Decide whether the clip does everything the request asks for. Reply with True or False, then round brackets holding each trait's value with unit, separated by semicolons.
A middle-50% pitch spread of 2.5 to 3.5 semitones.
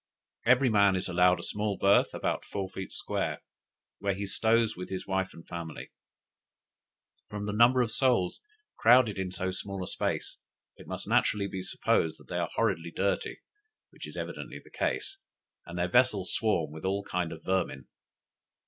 True (2.8 semitones)